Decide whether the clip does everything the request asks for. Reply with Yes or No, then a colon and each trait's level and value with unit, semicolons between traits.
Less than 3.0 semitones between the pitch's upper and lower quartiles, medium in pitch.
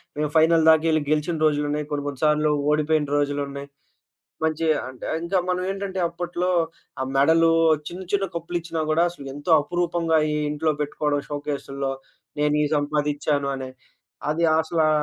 Yes: narrow, 2.4 semitones; medium, 155 Hz